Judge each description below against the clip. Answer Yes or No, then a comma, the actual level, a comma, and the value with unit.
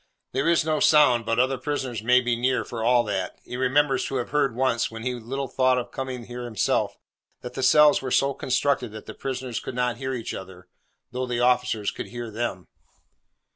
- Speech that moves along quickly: Yes, fast, 210 wpm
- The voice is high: No, low, 125 Hz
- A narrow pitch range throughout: Yes, narrow, 2.0 semitones